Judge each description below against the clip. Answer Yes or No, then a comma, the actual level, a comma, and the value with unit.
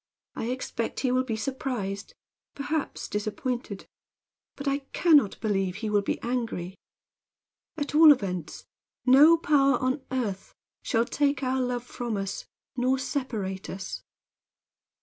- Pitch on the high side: Yes, very high, 250 Hz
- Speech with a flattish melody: No, average, 4.9 semitones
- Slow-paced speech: Yes, slow, 130 wpm